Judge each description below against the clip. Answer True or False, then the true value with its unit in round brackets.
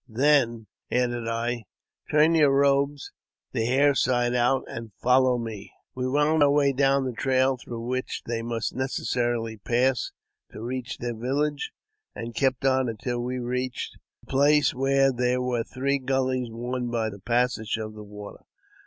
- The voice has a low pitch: True (125 Hz)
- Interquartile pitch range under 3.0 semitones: True (2.5 semitones)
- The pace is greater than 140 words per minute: True (160 wpm)